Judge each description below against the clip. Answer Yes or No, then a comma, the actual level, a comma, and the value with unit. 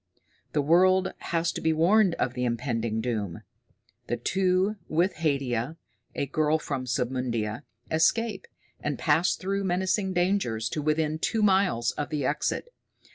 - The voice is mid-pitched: Yes, medium, 155 Hz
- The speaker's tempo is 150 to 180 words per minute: No, average, 140 wpm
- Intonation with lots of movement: Yes, wide, 6.9 semitones